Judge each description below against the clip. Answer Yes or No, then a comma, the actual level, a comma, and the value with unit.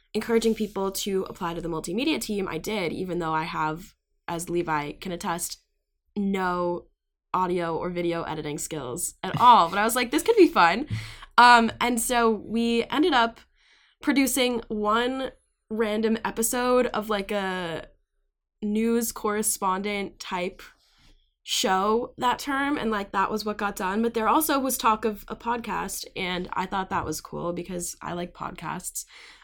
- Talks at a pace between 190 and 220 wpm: No, average, 160 wpm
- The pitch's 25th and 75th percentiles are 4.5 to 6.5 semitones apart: Yes, average, 4.8 semitones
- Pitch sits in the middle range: No, high, 210 Hz